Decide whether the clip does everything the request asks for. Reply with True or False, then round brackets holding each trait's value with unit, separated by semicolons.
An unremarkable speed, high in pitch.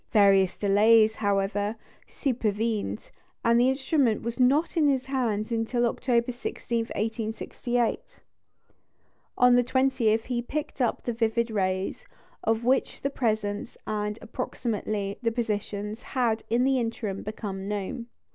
False (130 wpm; 225 Hz)